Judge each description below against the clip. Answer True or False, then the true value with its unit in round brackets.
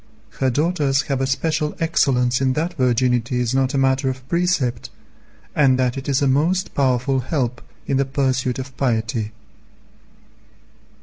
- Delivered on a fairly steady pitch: True (2.2 semitones)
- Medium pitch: False (130 Hz)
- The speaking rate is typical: True (150 wpm)